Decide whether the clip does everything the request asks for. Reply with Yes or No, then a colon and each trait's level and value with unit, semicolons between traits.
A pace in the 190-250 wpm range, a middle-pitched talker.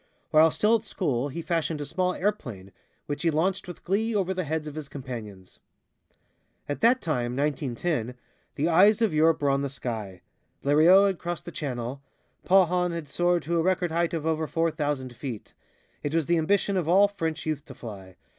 Yes: average, 195 wpm; medium, 160 Hz